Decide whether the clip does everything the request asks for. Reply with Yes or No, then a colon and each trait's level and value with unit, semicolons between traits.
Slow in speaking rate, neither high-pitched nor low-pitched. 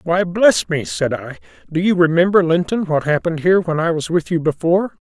No: average, 200 wpm; medium, 170 Hz